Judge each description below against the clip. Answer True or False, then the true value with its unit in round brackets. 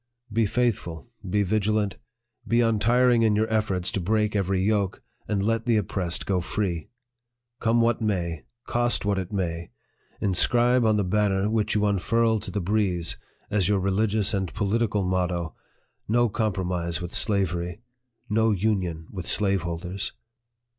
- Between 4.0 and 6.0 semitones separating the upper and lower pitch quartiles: False (3.2 semitones)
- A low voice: True (100 Hz)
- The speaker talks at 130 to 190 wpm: True (145 wpm)